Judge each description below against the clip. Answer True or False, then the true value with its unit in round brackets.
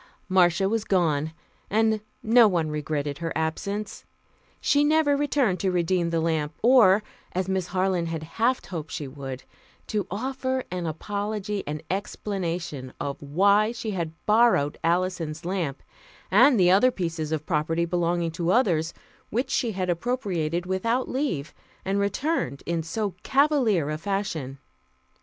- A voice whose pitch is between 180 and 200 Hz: True (185 Hz)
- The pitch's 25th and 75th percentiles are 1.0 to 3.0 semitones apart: False (4.8 semitones)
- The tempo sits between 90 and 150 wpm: True (145 wpm)